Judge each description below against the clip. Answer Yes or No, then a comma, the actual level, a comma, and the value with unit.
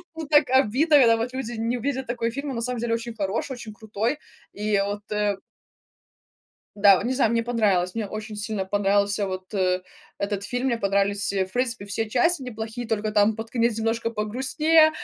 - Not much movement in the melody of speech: No, average, 3.3 semitones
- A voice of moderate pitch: No, high, 225 Hz